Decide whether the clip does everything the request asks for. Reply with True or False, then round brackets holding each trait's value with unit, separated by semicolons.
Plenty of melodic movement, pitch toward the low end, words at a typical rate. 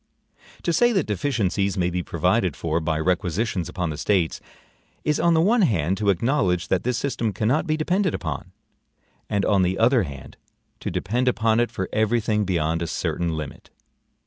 True (6.1 semitones; 100 Hz; 180 wpm)